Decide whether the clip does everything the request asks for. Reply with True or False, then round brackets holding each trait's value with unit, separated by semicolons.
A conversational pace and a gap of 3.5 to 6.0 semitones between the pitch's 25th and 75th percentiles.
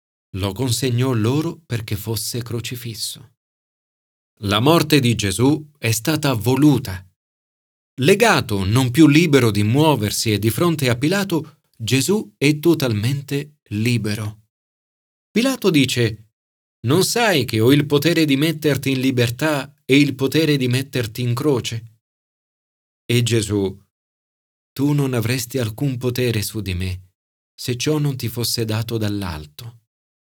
True (125 wpm; 5.1 semitones)